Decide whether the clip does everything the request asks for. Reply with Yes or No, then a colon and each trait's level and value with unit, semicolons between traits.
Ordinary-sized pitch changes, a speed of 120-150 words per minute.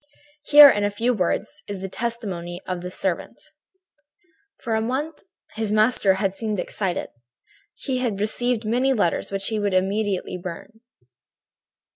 Yes: average, 3.6 semitones; average, 145 wpm